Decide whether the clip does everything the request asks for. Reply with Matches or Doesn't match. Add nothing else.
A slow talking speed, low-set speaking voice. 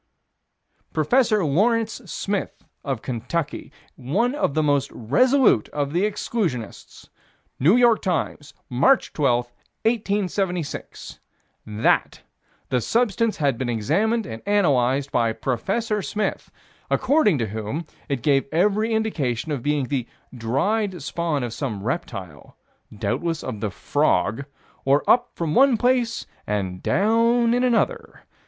Doesn't match